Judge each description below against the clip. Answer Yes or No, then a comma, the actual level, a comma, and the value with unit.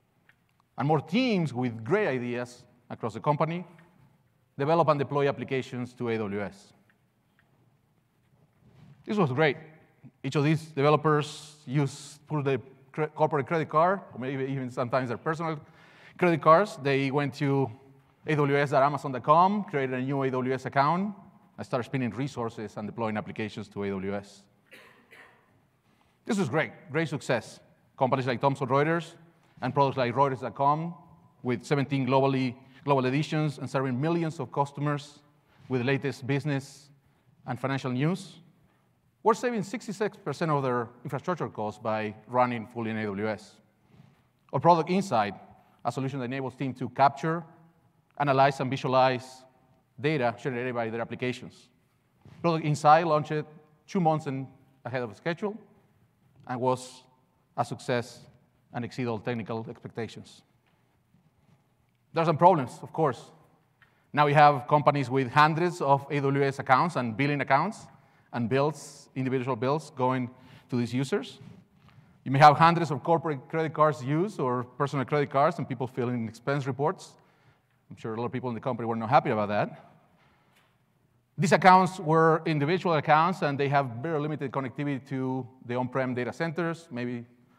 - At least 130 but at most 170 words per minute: Yes, average, 140 wpm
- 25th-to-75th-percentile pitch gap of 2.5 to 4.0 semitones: Yes, average, 3.5 semitones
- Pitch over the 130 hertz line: Yes, medium, 140 Hz